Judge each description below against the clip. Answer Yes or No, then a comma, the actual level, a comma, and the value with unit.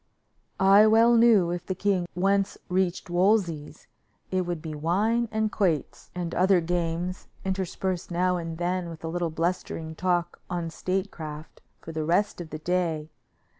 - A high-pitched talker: No, medium, 175 Hz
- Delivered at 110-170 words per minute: Yes, average, 155 wpm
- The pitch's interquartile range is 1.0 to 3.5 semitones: Yes, narrow, 2.4 semitones